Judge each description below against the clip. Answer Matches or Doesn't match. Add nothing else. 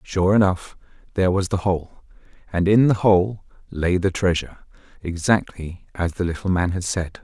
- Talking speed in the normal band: Matches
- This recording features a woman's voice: Doesn't match